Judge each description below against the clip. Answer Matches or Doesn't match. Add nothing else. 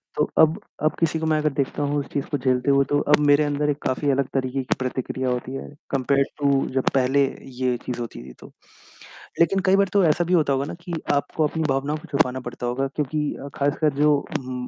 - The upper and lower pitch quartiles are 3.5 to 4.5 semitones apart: Doesn't match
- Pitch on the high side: Doesn't match